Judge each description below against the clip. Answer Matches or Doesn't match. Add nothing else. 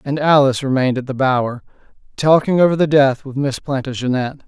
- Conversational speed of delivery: Matches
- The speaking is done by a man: Matches